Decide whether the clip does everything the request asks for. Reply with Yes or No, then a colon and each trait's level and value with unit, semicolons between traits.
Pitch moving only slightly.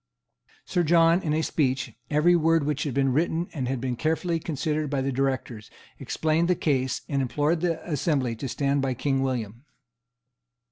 No: average, 3.5 semitones